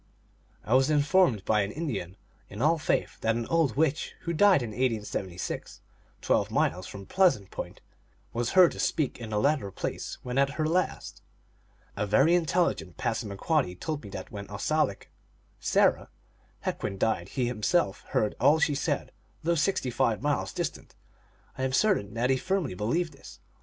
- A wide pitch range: Yes, wide, 7.1 semitones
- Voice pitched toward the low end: Yes, low, 130 Hz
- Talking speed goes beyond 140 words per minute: Yes, average, 165 wpm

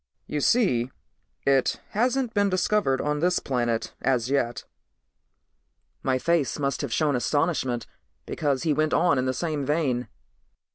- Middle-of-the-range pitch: Yes, medium, 145 Hz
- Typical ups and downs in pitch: Yes, average, 4.7 semitones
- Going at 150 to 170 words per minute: No, average, 140 wpm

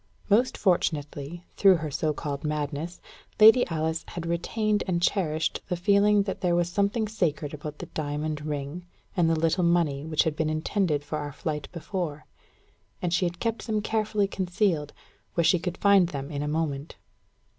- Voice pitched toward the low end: No, medium, 170 Hz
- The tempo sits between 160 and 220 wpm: Yes, average, 175 wpm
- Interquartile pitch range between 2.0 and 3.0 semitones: No, average, 4.2 semitones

